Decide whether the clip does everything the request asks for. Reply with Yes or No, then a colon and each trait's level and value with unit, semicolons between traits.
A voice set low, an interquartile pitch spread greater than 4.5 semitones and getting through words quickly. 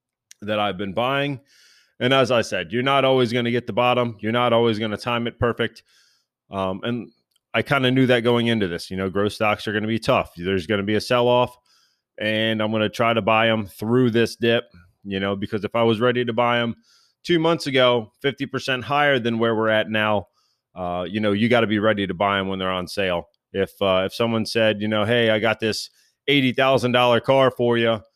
No: low, 115 Hz; average, 2.7 semitones; fast, 235 wpm